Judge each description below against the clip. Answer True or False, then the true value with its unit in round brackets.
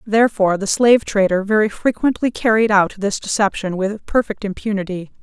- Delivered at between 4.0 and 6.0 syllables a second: True (5.6 syllables/s)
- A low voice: False (205 Hz)